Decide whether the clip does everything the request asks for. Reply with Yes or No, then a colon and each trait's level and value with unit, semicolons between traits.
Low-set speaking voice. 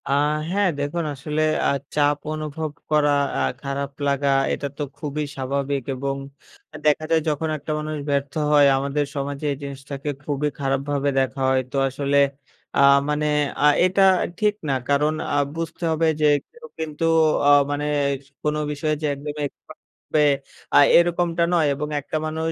No: medium, 145 Hz